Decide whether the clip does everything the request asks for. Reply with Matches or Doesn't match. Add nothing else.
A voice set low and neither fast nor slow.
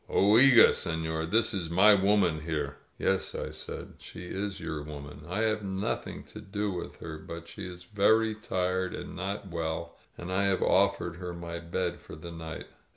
Matches